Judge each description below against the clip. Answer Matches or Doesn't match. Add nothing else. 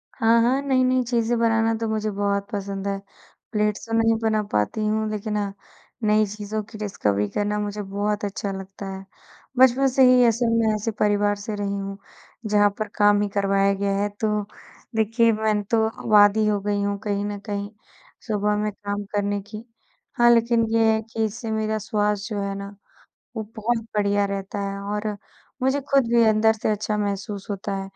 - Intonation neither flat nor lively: Doesn't match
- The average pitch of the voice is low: Doesn't match